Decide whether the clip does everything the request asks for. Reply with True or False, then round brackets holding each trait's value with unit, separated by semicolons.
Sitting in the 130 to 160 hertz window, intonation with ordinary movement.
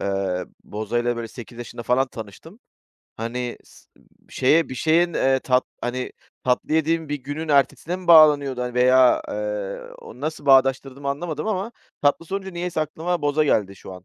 True (135 Hz; 4.6 semitones)